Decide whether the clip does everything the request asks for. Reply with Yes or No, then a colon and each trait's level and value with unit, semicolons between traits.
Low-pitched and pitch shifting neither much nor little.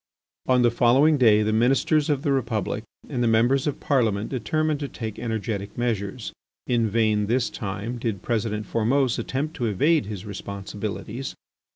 Yes: low, 115 Hz; average, 3.8 semitones